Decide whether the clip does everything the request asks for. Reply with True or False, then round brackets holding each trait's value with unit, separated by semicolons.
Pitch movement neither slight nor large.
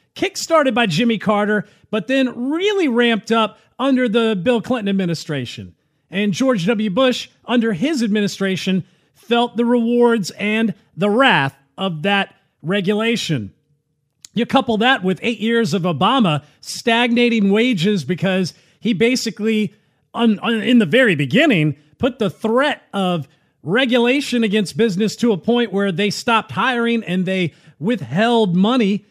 True (4.3 semitones)